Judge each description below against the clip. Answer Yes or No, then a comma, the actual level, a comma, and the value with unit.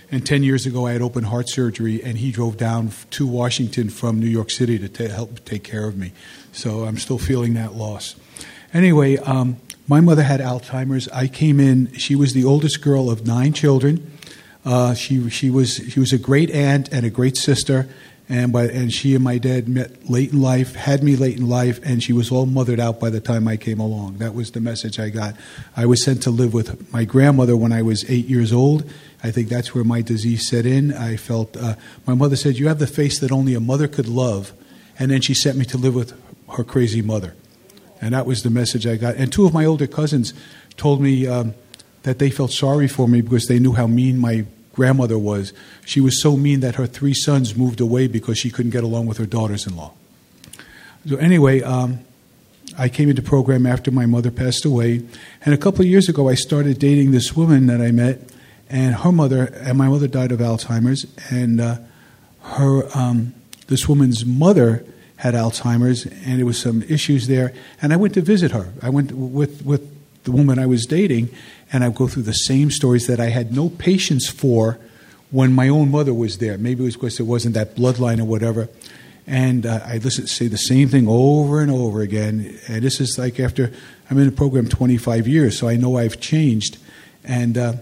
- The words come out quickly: Yes, fast, 220 wpm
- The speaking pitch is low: Yes, low, 125 Hz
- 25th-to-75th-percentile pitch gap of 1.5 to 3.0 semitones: Yes, narrow, 2.6 semitones